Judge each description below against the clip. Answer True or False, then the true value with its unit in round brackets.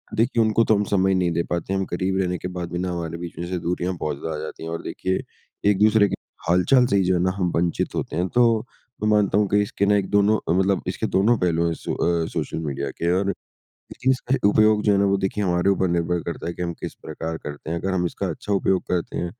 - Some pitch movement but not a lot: True (3.0 semitones)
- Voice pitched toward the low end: True (95 Hz)